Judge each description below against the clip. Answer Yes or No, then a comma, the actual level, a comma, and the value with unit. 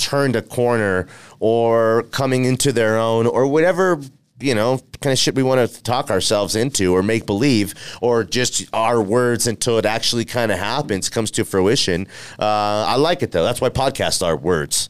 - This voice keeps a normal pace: Yes, average, 190 wpm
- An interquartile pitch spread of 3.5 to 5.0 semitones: No, average, 3.1 semitones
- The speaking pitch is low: Yes, low, 115 Hz